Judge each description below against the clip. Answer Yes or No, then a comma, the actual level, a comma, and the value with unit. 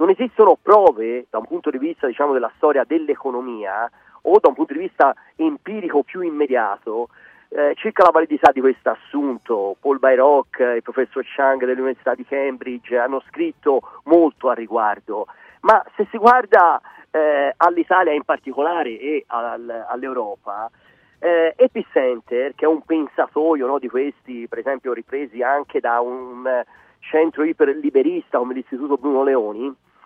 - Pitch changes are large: Yes, wide, 7.5 semitones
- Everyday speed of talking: Yes, average, 140 wpm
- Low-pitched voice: No, medium, 145 Hz